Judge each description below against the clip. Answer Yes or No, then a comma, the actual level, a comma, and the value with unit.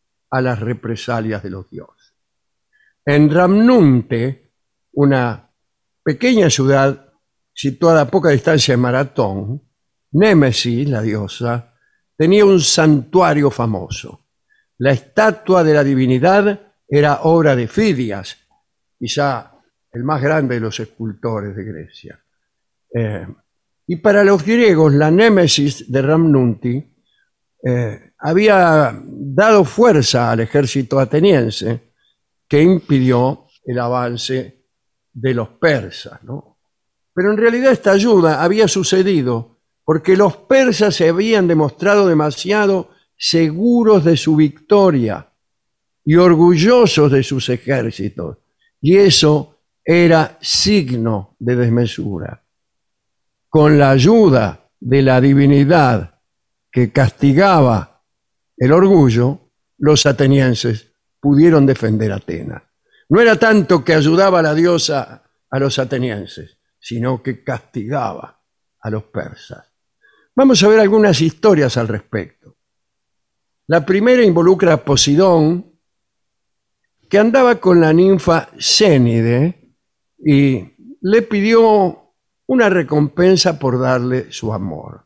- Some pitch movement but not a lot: No, wide, 6.8 semitones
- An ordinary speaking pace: No, slow, 110 wpm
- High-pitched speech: No, medium, 140 Hz